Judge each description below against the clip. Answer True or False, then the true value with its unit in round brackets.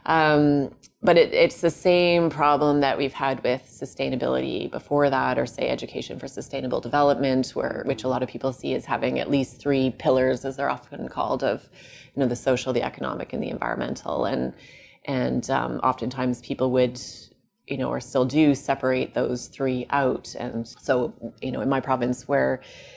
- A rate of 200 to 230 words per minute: False (185 wpm)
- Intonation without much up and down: True (2.1 semitones)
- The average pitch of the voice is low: True (130 Hz)